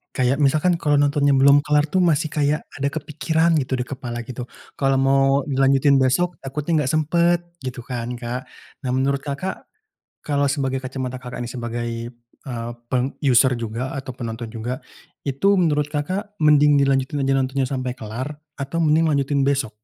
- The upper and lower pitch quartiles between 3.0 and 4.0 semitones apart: No, narrow, 2.6 semitones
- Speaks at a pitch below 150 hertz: Yes, low, 135 Hz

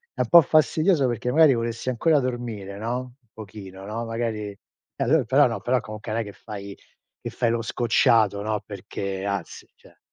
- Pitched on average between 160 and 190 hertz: No, low, 115 Hz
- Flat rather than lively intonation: No, average, 3.6 semitones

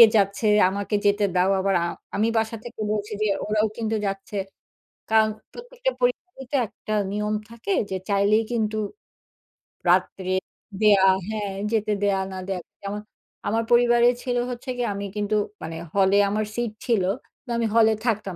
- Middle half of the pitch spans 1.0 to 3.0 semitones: Yes, narrow, 2.5 semitones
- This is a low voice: No, high, 215 Hz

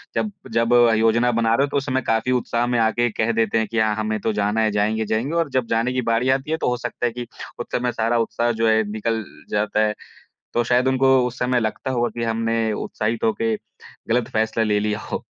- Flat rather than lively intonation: Yes, narrow, 1.9 semitones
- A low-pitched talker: Yes, low, 115 Hz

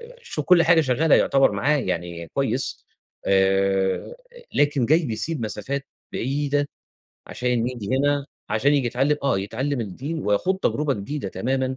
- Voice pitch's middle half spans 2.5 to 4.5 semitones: No, average, 5.0 semitones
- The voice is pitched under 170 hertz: Yes, low, 135 Hz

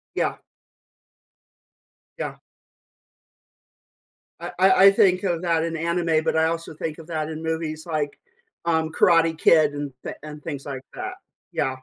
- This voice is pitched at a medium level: Yes, medium, 160 Hz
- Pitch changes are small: Yes, narrow, 1.5 semitones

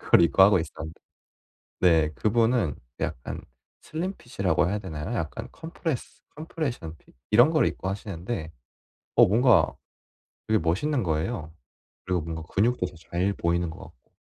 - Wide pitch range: Yes, wide, 6.6 semitones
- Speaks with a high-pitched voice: No, very low, 95 Hz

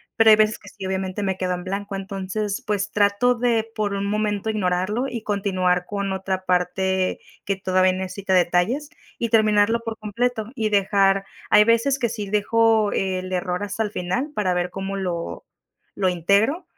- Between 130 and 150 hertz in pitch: No, high, 200 Hz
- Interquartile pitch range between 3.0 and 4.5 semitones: No, narrow, 2.5 semitones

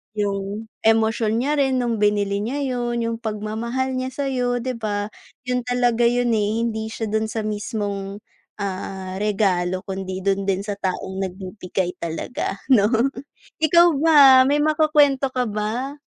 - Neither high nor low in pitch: No, high, 220 Hz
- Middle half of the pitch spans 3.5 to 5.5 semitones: Yes, average, 3.8 semitones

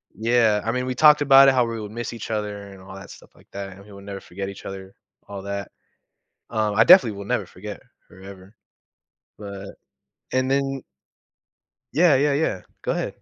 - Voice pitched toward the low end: Yes, low, 105 Hz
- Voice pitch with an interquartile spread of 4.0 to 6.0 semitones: Yes, average, 4.3 semitones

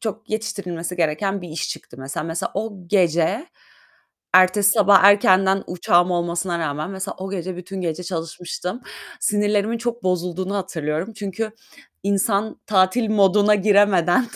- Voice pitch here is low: No, high, 190 Hz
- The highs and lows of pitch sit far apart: No, average, 2.9 semitones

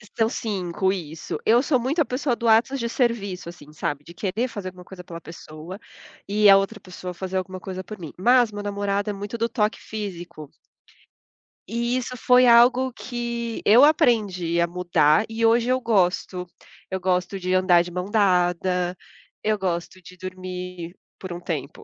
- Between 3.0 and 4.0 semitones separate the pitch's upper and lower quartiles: No, average, 4.4 semitones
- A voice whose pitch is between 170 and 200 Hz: Yes, high, 195 Hz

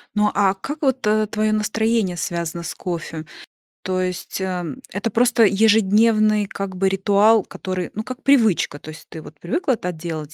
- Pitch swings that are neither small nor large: Yes, average, 3.6 semitones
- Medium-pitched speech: No, high, 200 Hz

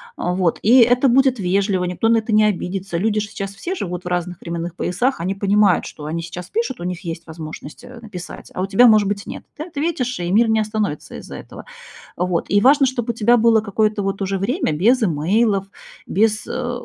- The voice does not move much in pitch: No, average, 4.6 semitones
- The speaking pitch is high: Yes, high, 205 Hz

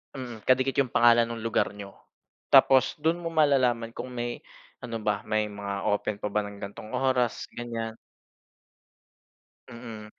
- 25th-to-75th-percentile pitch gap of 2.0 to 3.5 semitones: Yes, average, 3.1 semitones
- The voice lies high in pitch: No, low, 115 Hz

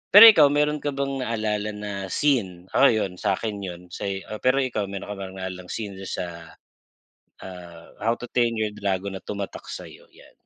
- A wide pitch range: No, average, 4.4 semitones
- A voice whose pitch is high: No, low, 105 Hz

